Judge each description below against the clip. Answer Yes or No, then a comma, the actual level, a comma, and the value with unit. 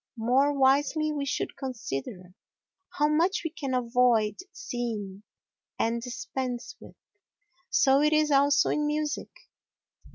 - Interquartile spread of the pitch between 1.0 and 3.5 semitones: No, average, 3.9 semitones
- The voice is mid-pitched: No, very high, 265 Hz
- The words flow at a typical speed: No, slow, 120 wpm